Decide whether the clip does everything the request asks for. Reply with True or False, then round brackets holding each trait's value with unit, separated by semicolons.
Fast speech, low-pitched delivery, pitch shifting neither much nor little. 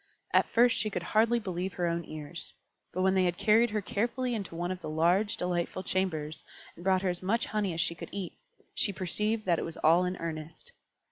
False (220 wpm; 185 Hz; 3.7 semitones)